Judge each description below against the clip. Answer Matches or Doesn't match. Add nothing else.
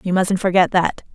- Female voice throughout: Matches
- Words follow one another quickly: Matches